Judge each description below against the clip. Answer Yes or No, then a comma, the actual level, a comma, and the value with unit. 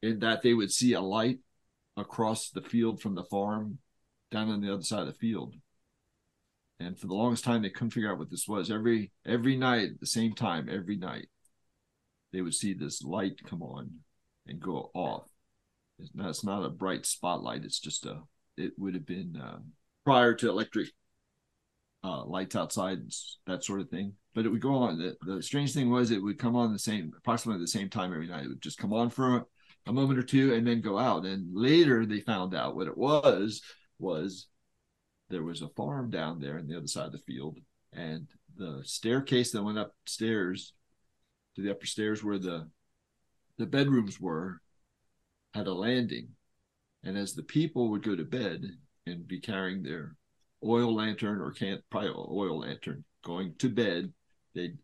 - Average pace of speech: Yes, average, 195 wpm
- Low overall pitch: Yes, low, 110 Hz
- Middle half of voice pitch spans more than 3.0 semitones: Yes, average, 3.9 semitones